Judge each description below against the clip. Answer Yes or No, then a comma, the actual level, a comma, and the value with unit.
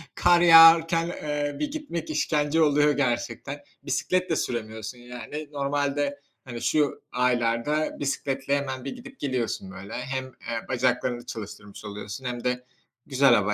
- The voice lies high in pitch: No, low, 135 Hz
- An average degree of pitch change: Yes, average, 3.7 semitones